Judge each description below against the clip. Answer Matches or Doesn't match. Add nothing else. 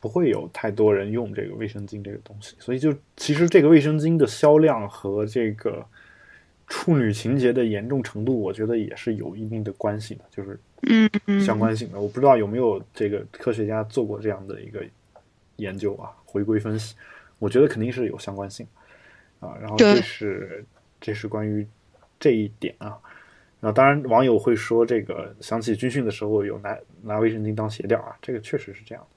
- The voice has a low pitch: Matches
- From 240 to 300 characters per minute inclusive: Matches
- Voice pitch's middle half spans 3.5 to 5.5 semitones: Doesn't match